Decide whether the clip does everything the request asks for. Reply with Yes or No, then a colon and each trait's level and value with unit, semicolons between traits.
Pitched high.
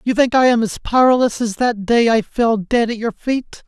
Yes: high, 230 Hz